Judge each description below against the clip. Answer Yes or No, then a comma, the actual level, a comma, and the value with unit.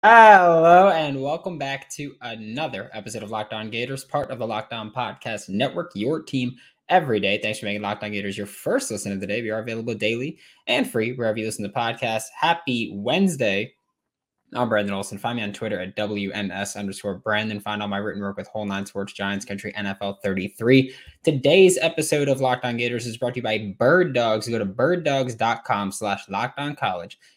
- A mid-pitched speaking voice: No, low, 110 Hz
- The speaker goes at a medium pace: Yes, average, 185 wpm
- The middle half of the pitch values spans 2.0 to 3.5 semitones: No, average, 4.6 semitones